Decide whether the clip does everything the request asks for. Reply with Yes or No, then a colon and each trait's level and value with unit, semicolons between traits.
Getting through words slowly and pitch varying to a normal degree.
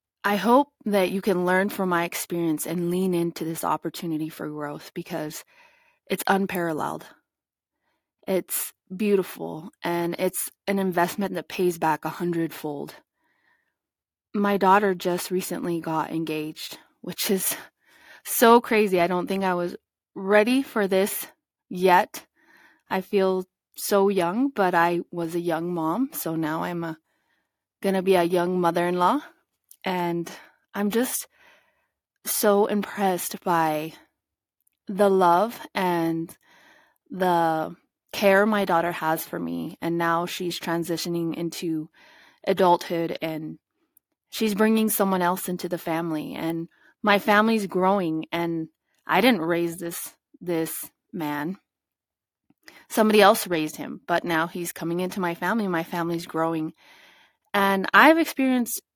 Yes: slow, 130 wpm; average, 3.4 semitones